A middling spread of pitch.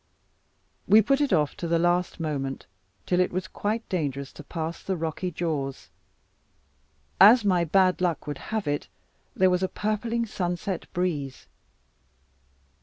Yes: average, 3.7 semitones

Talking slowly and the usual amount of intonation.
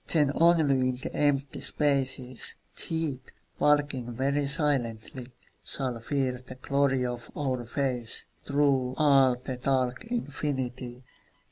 No: slow, 115 wpm; narrow, 2.3 semitones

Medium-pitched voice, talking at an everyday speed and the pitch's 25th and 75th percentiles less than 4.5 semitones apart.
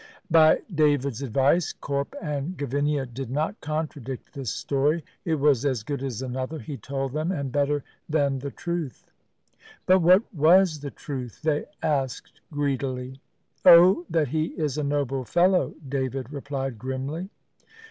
Yes: medium, 145 Hz; average, 145 wpm; average, 2.8 semitones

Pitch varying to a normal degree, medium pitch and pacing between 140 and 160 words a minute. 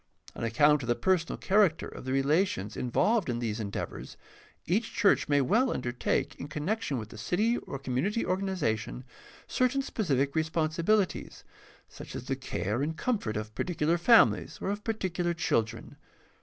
No: wide, 8.1 semitones; medium, 155 Hz; average, 155 wpm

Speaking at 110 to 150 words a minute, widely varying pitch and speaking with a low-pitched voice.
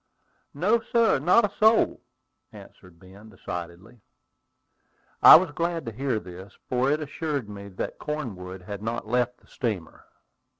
Yes: average, 140 wpm; wide, 7.7 semitones; low, 120 Hz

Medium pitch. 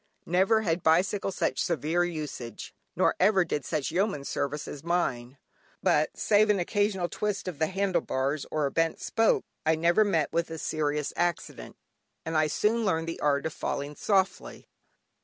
Yes: medium, 165 Hz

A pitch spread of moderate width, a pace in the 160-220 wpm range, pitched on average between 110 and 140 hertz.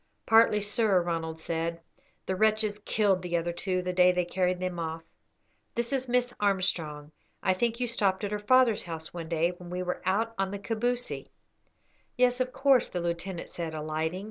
No: average, 4.4 semitones; average, 185 wpm; medium, 185 Hz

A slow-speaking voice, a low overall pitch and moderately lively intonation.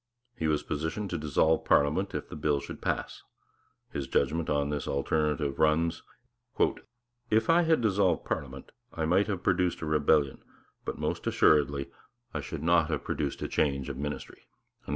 No: average, 160 wpm; very low, 80 Hz; average, 3.1 semitones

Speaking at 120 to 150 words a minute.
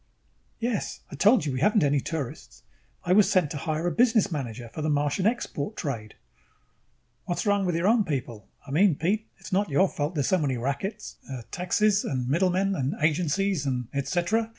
No: average, 200 wpm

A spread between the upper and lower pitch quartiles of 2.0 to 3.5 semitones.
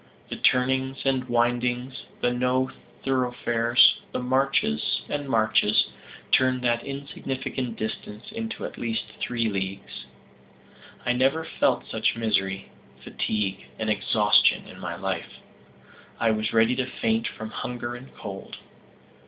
Yes: average, 2.9 semitones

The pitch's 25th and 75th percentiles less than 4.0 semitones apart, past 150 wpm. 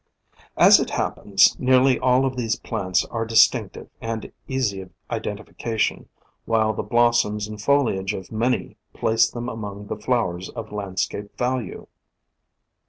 No: average, 2.9 semitones; average, 145 wpm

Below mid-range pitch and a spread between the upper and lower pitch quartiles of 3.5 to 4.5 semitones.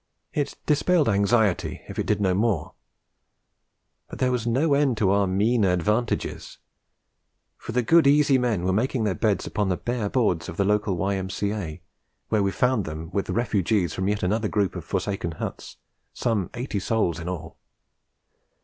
Yes: low, 105 Hz; average, 4.1 semitones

